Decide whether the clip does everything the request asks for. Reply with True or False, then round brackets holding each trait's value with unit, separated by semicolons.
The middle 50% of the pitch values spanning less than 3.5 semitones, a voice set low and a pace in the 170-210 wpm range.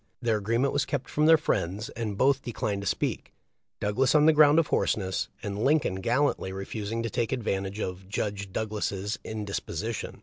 False (5.0 semitones; 110 Hz; 180 wpm)